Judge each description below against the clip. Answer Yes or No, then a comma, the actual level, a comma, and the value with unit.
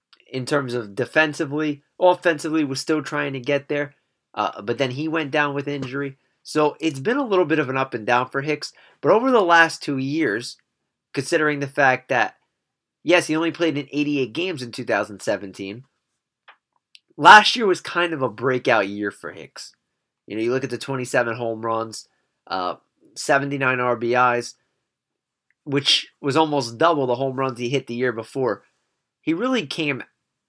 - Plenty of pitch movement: No, average, 3.7 semitones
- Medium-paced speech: Yes, average, 175 wpm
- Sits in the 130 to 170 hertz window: Yes, medium, 140 Hz